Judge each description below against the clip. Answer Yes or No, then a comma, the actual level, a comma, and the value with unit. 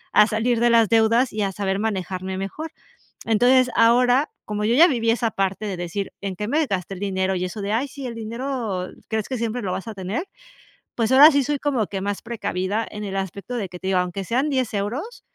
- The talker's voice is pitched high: Yes, high, 220 Hz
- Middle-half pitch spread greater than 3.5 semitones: Yes, average, 4.1 semitones